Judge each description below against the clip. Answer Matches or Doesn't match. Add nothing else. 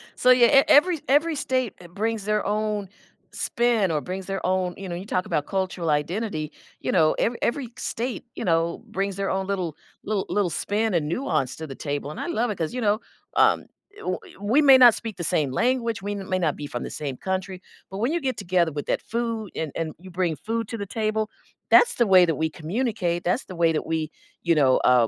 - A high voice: Matches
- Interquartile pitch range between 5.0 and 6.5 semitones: Matches